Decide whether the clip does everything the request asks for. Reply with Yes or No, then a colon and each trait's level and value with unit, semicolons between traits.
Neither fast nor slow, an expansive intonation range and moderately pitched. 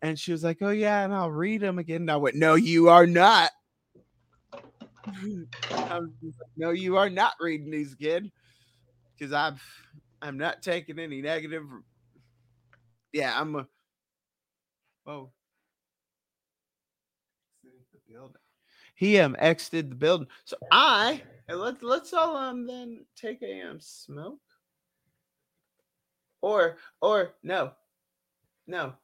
No: slow, 125 wpm; wide, 5.7 semitones; medium, 165 Hz